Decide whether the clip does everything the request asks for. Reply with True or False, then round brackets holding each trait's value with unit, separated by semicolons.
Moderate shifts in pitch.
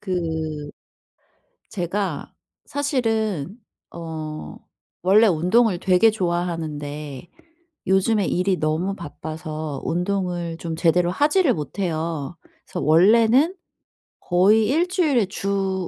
True (4.8 semitones)